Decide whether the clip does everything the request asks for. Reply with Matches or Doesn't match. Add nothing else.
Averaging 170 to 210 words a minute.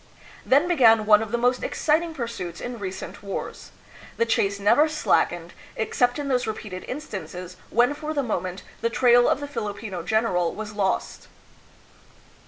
Doesn't match